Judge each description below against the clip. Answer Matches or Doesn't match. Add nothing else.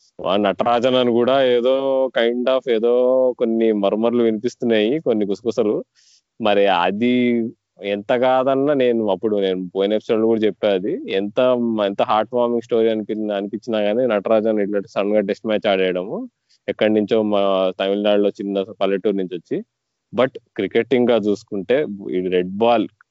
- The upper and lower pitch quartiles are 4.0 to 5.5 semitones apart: Doesn't match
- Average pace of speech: Doesn't match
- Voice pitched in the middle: Doesn't match